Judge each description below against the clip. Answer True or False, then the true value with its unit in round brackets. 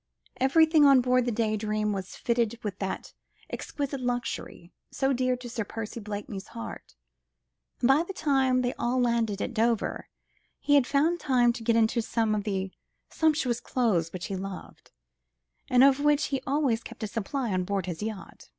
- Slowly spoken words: False (180 wpm)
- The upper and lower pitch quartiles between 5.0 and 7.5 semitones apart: False (4.0 semitones)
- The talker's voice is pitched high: True (235 Hz)